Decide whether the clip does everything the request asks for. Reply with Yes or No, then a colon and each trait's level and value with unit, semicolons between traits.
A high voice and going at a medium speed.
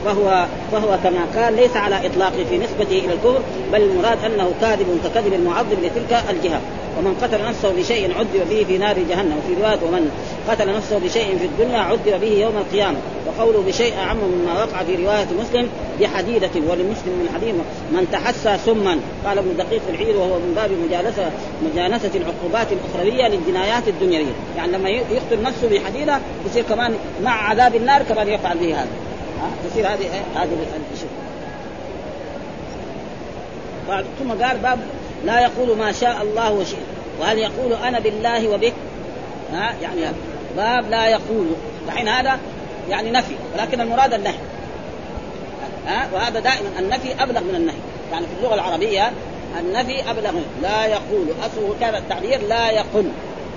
No: high, 220 Hz; fast, 150 wpm